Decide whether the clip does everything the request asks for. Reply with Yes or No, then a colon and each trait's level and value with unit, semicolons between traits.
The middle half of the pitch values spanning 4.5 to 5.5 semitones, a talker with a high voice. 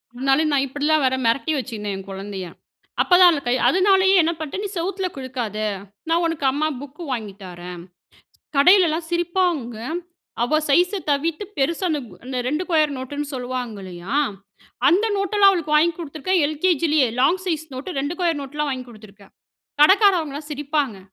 Yes: average, 5.0 semitones; very high, 295 Hz